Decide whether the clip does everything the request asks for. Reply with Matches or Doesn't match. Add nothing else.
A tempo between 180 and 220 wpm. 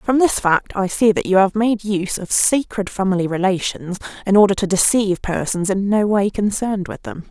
Matches